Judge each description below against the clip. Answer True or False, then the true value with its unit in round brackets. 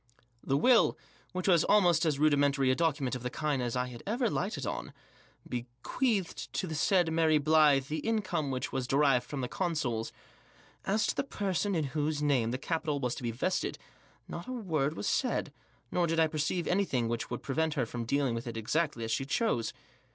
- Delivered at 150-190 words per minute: False (205 wpm)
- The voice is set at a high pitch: False (150 Hz)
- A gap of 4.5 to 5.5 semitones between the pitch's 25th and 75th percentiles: True (5.1 semitones)